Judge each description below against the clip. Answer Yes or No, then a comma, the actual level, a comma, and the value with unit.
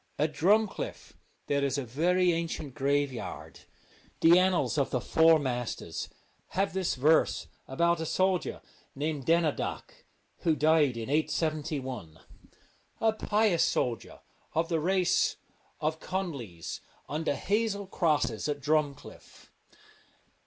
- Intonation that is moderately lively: Yes, average, 4.0 semitones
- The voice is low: No, medium, 155 Hz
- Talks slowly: Yes, slow, 115 wpm